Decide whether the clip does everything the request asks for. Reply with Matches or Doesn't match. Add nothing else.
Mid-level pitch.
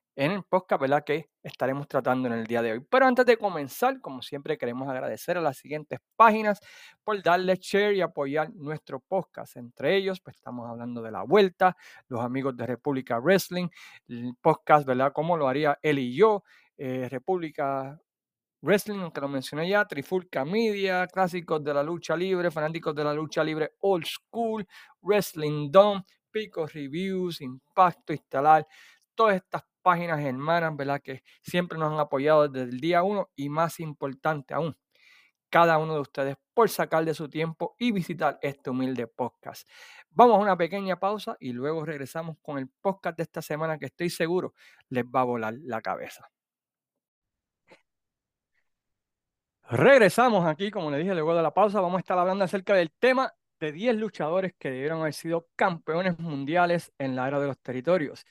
Matches